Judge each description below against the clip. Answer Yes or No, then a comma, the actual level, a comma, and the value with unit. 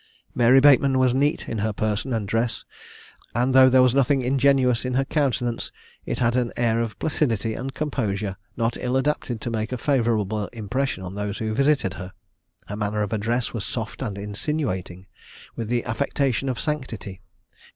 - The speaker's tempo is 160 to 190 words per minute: Yes, average, 175 wpm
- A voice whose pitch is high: No, low, 120 Hz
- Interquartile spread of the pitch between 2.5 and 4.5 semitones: Yes, average, 3.6 semitones